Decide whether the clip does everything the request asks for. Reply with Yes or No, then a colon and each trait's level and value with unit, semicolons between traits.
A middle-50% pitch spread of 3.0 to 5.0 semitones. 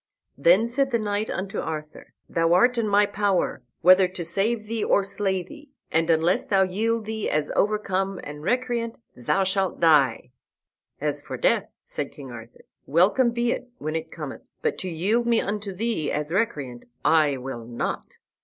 No: wide, 5.5 semitones